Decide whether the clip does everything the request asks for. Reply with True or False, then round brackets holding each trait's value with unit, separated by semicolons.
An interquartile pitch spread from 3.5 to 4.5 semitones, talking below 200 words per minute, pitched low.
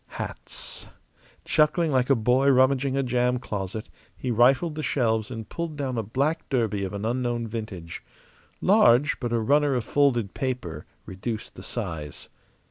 True (3.9 semitones; 155 wpm; 125 Hz)